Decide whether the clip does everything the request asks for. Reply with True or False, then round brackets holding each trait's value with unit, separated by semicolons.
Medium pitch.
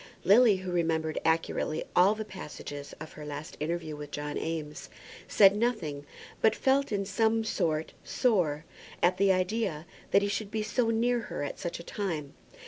True (180 Hz)